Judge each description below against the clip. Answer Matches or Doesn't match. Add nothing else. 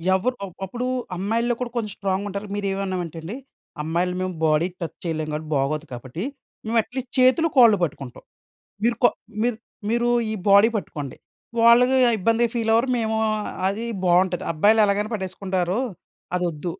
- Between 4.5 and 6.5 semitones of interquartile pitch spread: Matches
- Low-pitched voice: Doesn't match